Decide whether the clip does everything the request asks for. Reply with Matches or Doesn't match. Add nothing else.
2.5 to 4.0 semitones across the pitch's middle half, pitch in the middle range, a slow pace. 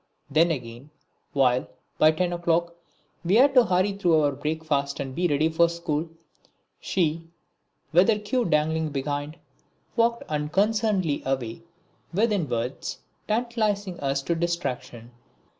Doesn't match